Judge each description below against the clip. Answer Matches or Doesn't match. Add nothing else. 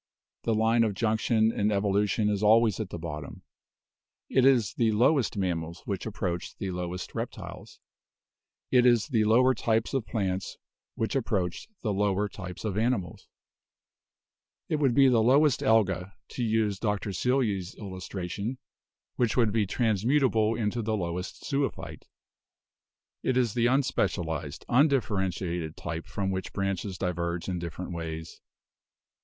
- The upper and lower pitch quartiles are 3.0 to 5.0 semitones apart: Matches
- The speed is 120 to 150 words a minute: Matches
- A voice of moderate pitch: Doesn't match